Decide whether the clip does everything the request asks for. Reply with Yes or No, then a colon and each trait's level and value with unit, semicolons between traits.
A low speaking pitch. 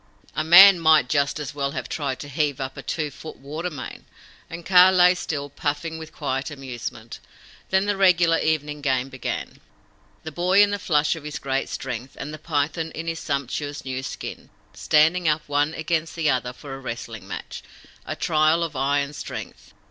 No: medium, 150 Hz